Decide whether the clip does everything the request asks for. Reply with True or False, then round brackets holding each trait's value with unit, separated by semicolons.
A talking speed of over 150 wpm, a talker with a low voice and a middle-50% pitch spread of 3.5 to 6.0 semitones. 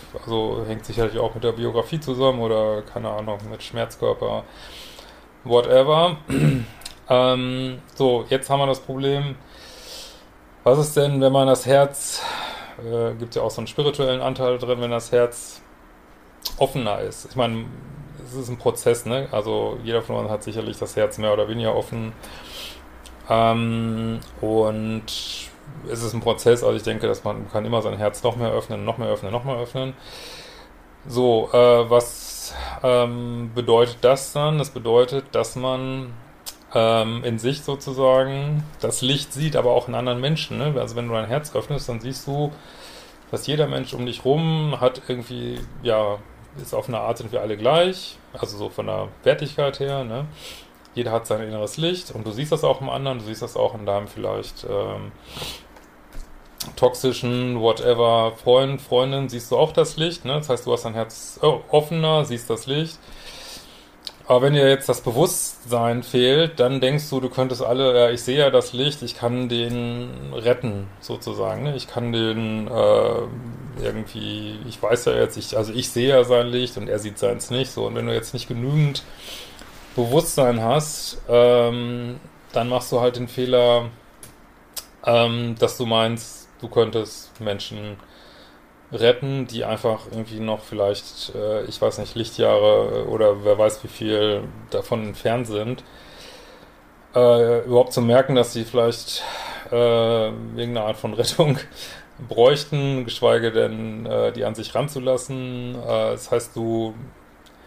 False (165 wpm; 120 Hz; 3.0 semitones)